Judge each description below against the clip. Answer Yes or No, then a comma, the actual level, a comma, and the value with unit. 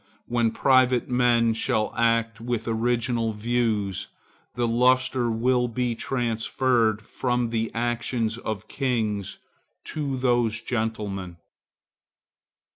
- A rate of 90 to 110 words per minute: Yes, slow, 105 wpm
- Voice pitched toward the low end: Yes, low, 115 Hz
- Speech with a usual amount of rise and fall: No, narrow, 1.7 semitones